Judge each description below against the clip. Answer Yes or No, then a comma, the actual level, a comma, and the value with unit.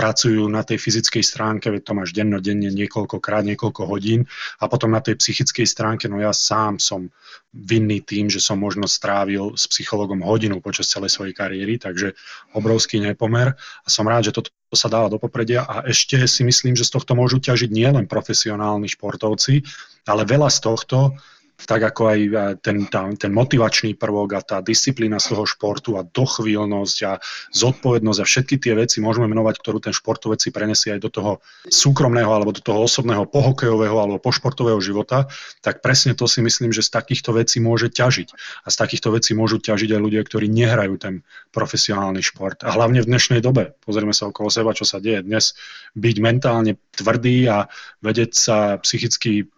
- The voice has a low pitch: Yes, low, 110 Hz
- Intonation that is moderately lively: No, narrow, 2.1 semitones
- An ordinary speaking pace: No, fast, 180 wpm